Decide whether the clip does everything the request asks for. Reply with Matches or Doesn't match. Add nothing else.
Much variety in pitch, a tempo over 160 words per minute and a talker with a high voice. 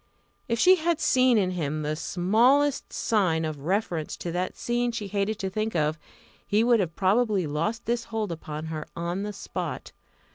Matches